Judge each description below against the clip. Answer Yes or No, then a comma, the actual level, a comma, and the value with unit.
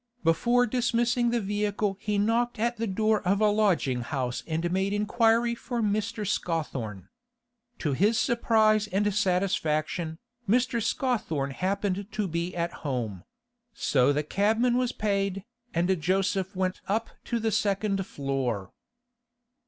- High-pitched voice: Yes, high, 200 Hz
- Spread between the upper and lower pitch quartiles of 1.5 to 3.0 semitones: No, average, 4.8 semitones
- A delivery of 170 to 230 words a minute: No, slow, 135 wpm